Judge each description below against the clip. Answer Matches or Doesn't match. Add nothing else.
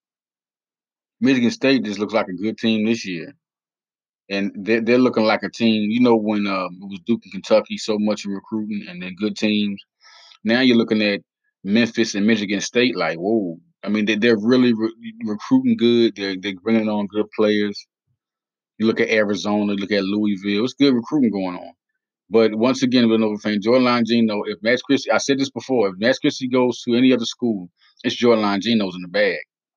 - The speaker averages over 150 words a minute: Matches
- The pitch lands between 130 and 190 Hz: Doesn't match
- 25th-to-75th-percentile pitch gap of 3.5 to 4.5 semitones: Doesn't match